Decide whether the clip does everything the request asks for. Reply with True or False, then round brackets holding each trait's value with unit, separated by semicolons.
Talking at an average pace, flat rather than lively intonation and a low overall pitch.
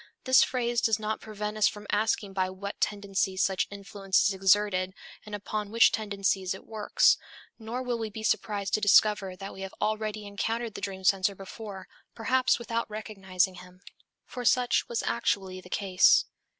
False (170 wpm; 2.2 semitones; 205 Hz)